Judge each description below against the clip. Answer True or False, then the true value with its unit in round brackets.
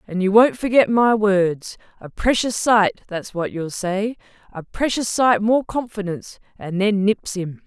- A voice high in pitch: True (205 Hz)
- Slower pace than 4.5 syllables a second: True (4.2 syllables/s)